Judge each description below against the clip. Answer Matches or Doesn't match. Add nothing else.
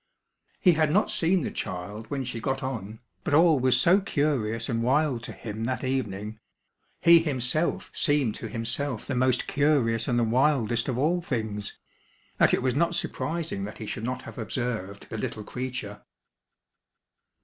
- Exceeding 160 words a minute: Matches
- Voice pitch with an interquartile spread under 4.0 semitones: Doesn't match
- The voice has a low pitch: Matches